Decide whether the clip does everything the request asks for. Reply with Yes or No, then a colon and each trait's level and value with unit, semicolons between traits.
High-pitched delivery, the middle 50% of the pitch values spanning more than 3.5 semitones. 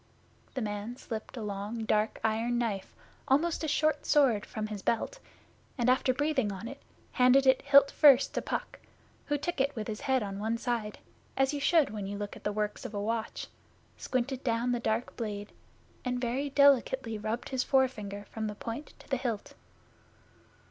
Yes: high, 240 Hz; average, 4.1 semitones